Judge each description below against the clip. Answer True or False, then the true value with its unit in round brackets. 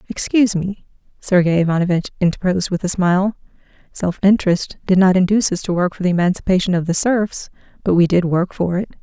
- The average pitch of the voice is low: False (185 Hz)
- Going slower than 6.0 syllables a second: False (6.3 syllables/s)